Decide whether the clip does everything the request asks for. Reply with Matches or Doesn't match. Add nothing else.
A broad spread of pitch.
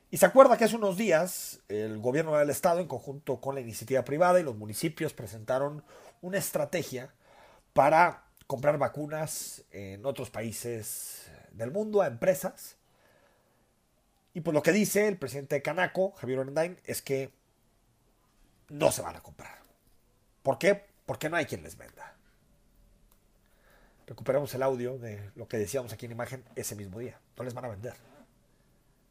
Matches